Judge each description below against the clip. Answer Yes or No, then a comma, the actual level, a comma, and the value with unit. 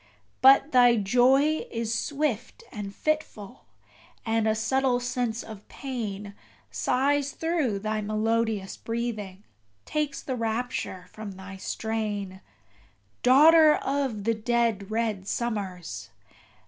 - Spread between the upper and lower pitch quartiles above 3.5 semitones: Yes, average, 4.1 semitones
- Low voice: No, high, 230 Hz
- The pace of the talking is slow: Yes, slow, 110 wpm